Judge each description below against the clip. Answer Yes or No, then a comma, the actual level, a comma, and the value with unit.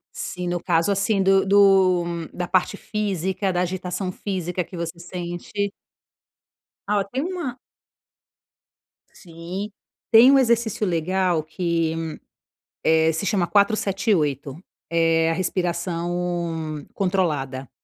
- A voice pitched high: No, medium, 180 Hz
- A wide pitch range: No, average, 2.9 semitones